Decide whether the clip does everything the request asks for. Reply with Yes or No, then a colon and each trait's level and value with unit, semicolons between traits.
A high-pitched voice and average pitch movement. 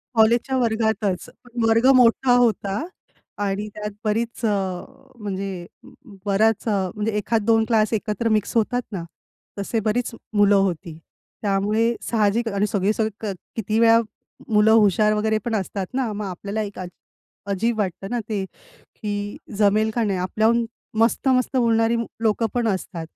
No: high, 215 Hz; narrow, 2.3 semitones